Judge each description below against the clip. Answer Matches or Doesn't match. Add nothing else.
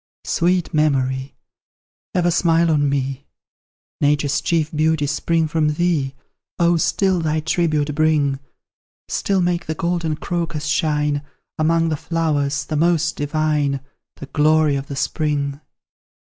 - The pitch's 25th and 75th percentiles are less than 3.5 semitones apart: Matches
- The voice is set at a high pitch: Doesn't match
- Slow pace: Matches